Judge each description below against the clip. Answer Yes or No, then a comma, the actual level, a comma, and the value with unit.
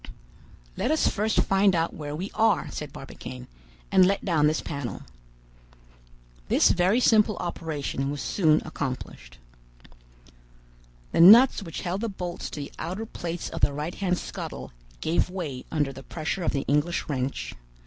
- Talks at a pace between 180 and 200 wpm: No, average, 155 wpm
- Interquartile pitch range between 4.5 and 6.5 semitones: Yes, average, 4.8 semitones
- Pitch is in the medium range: Yes, medium, 165 Hz